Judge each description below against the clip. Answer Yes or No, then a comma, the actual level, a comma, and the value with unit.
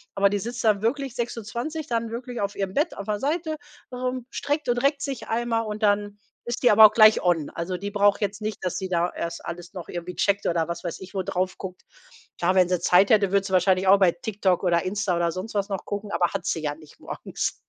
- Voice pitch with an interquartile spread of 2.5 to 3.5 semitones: No, average, 3.9 semitones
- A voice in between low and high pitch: No, high, 200 Hz